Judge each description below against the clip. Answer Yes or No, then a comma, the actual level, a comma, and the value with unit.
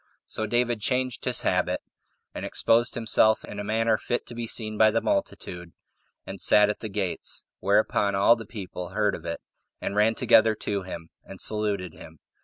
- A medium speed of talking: Yes, average, 185 wpm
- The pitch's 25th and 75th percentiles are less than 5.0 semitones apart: Yes, narrow, 2.4 semitones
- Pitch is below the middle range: Yes, low, 105 Hz